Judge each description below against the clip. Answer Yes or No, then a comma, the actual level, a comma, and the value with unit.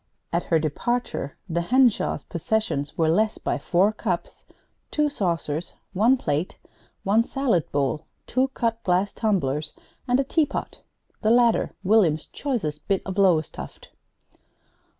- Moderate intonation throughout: No, wide, 6.6 semitones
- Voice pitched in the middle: No, high, 195 Hz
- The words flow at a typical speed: No, slow, 130 wpm